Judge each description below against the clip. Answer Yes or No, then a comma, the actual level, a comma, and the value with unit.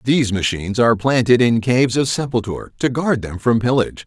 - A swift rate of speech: No, average, 190 wpm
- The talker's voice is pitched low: Yes, low, 120 Hz